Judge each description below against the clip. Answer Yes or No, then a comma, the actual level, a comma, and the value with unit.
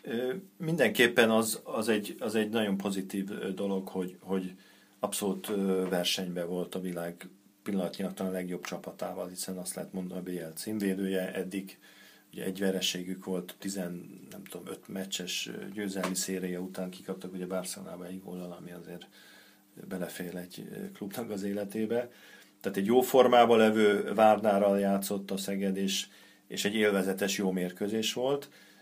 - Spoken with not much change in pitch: Yes, narrow, 1.9 semitones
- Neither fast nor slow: Yes, average, 145 wpm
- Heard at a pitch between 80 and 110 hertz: Yes, very low, 95 Hz